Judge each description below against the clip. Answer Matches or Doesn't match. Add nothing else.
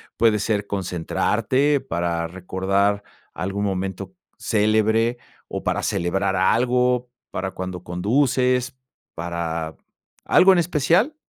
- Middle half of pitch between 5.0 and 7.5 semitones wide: Matches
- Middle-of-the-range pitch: Doesn't match